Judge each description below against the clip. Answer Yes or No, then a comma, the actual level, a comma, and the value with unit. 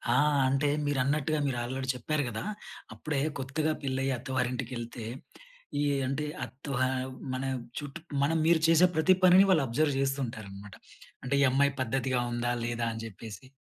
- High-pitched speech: No, low, 135 Hz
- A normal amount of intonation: Yes, average, 3.2 semitones